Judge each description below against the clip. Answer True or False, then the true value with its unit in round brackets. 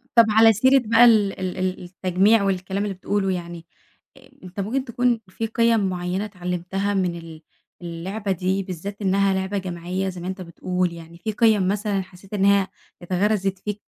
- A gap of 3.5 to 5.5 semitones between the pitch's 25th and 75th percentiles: False (2.4 semitones)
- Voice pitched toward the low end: False (190 Hz)